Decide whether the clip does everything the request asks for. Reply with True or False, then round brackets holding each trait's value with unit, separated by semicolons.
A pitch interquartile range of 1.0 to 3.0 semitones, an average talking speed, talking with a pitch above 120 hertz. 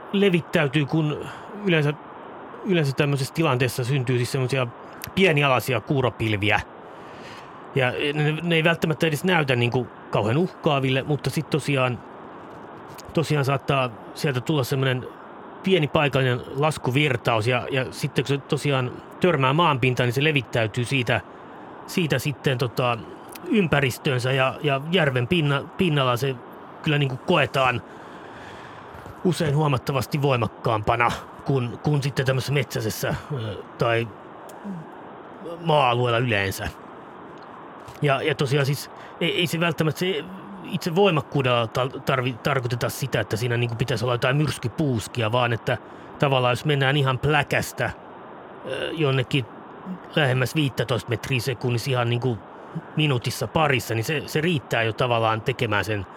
False (3.7 semitones; 125 wpm; 135 Hz)